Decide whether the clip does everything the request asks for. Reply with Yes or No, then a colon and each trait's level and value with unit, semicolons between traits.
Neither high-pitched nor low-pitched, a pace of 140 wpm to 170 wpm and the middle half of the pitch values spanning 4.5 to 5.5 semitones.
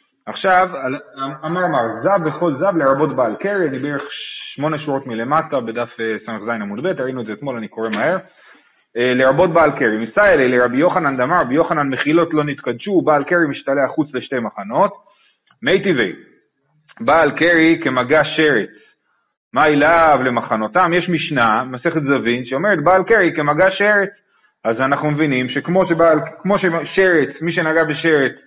Yes: medium, 150 Hz; fast, 150 wpm; average, 5.0 semitones